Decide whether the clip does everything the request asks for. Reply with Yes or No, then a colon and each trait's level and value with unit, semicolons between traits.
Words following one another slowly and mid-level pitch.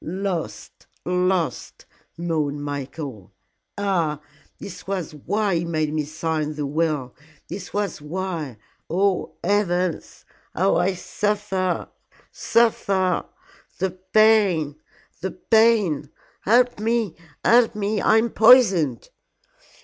Yes: slow, 105 wpm; medium, 180 Hz